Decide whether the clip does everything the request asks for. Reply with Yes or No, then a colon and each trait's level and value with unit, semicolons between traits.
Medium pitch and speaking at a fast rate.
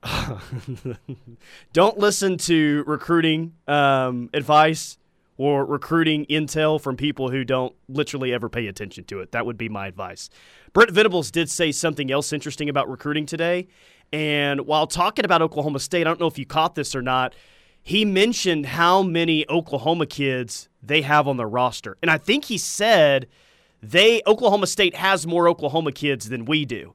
No: medium, 150 Hz; average, 165 wpm